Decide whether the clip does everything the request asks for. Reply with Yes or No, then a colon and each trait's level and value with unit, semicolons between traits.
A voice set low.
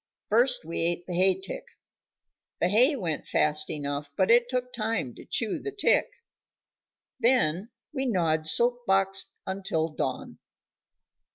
No: high, 195 Hz